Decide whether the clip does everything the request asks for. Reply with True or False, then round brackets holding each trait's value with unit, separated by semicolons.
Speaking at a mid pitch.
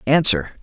False (120 Hz)